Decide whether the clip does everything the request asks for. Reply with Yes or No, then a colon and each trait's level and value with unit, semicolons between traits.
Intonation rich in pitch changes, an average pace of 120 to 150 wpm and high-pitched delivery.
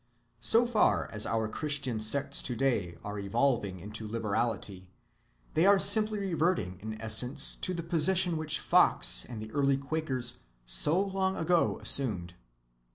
No: wide, 7.5 semitones; average, 140 wpm; low, 130 Hz